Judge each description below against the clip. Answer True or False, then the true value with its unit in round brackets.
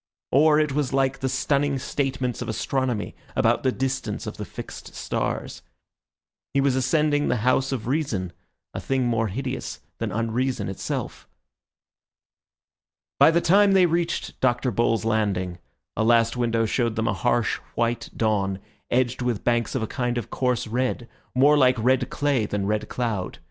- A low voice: True (125 Hz)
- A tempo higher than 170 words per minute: False (160 wpm)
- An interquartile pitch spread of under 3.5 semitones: True (3.0 semitones)